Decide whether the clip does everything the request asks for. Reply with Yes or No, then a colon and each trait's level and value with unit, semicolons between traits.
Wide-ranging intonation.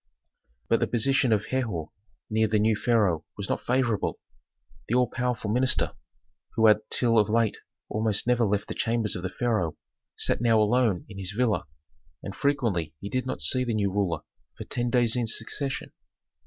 No: average, 3.1 semitones